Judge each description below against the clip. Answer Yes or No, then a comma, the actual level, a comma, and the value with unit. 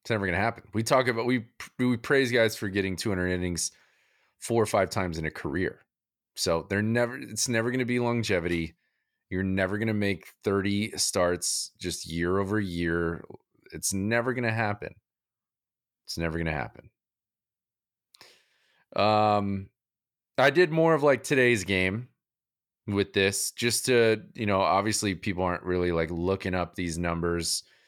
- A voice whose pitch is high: No, low, 100 Hz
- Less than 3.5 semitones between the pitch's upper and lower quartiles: No, average, 4.5 semitones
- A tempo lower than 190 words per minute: Yes, average, 165 wpm